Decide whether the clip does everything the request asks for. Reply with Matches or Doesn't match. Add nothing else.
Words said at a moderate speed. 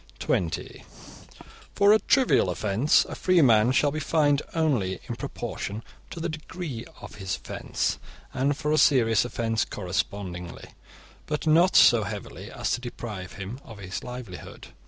Matches